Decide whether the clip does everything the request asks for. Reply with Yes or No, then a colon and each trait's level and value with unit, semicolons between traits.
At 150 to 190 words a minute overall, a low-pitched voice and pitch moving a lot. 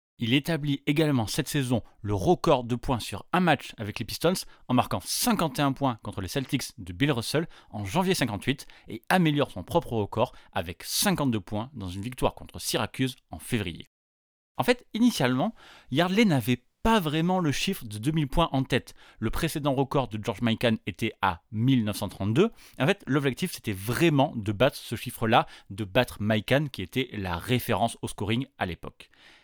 Yes: average, 175 wpm; low, 125 Hz; wide, 5.8 semitones